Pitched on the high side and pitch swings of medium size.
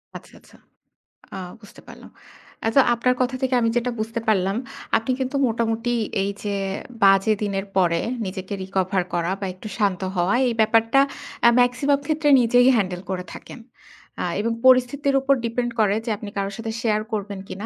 Yes: high, 220 Hz; average, 4.0 semitones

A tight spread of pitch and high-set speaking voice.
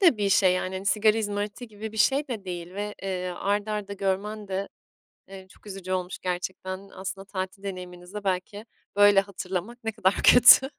Yes: narrow, 1.9 semitones; high, 195 Hz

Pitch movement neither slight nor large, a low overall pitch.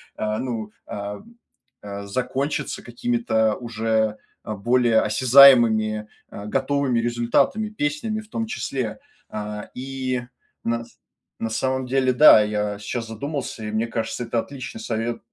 Yes: average, 3.4 semitones; low, 120 Hz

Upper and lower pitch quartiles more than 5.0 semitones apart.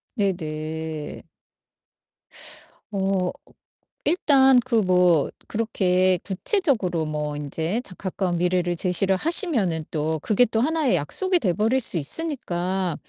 Yes: wide, 5.6 semitones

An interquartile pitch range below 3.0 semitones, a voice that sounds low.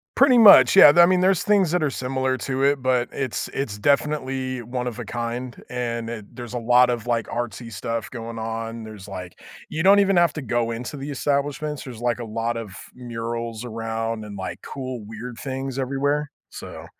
No: average, 3.4 semitones; low, 125 Hz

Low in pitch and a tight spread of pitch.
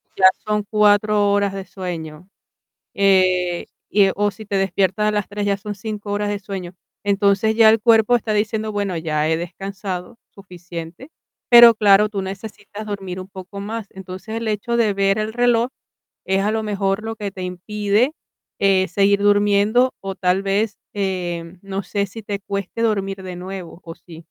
No: high, 200 Hz; narrow, 2.0 semitones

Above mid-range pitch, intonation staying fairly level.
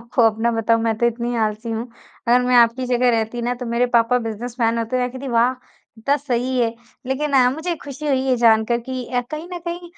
Yes: high, 245 Hz; narrow, 2.1 semitones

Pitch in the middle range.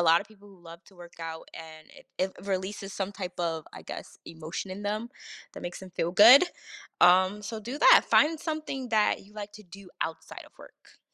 No: high, 195 Hz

